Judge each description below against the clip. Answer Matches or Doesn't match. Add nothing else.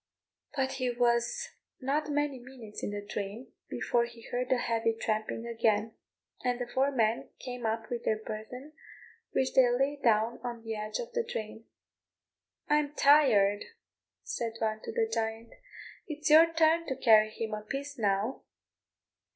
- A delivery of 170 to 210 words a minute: Doesn't match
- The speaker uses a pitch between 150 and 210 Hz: Doesn't match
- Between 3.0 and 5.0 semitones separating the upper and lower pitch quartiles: Matches